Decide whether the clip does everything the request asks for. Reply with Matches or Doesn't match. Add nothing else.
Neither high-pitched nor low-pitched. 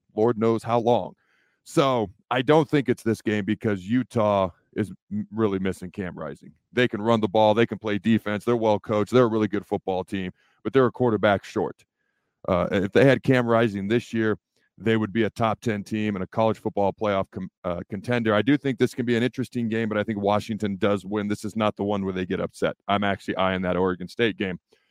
Doesn't match